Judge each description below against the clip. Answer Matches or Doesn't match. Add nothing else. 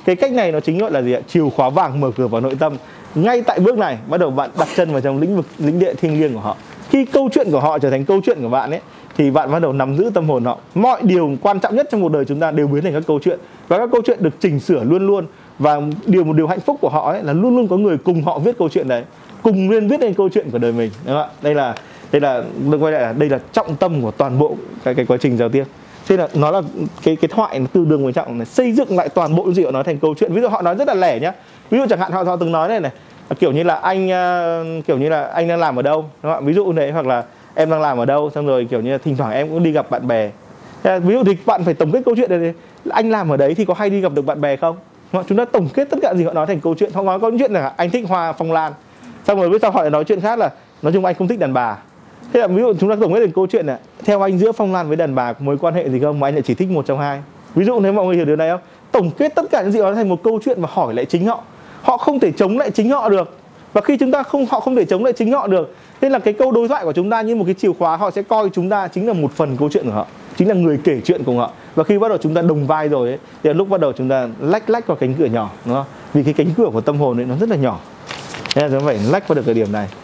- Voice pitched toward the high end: Doesn't match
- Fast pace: Matches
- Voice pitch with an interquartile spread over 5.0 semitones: Matches